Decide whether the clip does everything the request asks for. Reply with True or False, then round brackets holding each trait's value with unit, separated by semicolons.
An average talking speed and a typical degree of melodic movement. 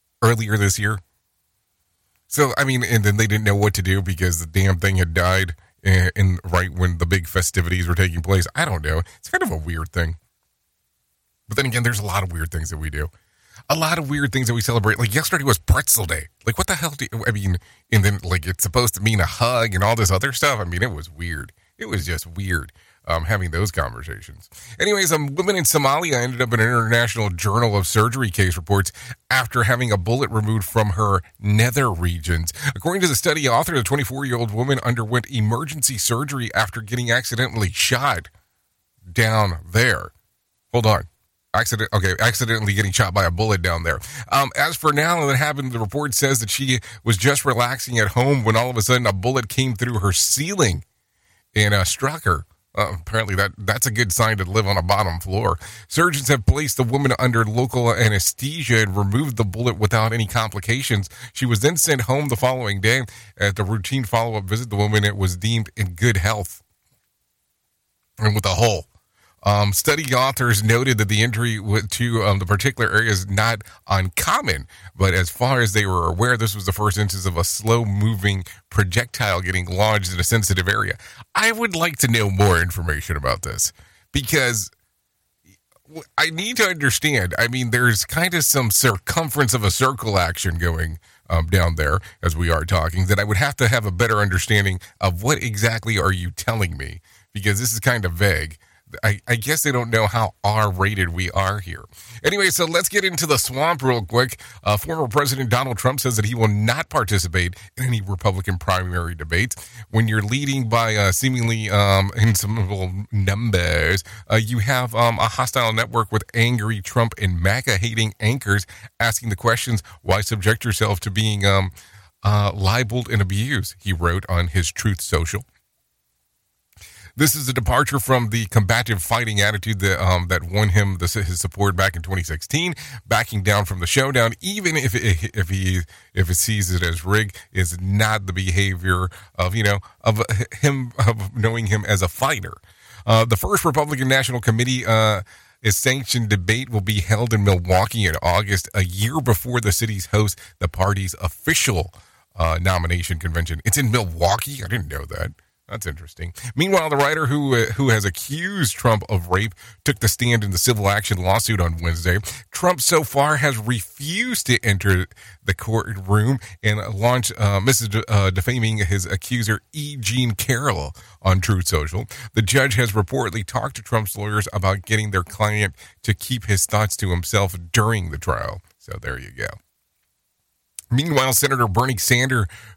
True (185 wpm; 4.2 semitones)